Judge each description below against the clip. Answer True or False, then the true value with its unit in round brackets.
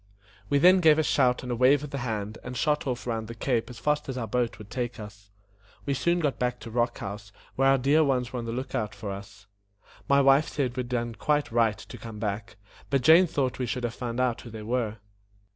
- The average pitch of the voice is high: False (125 Hz)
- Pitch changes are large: False (3.5 semitones)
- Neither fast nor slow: False (250 wpm)